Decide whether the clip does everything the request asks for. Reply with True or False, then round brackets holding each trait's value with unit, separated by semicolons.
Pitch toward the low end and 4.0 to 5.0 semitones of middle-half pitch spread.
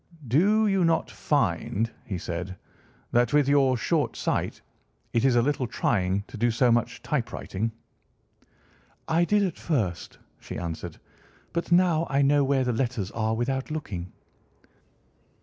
False (125 Hz; 5.5 semitones)